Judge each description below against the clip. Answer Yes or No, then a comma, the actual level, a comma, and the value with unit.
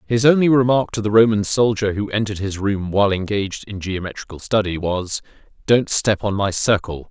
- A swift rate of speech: No, average, 185 wpm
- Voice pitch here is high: No, low, 105 Hz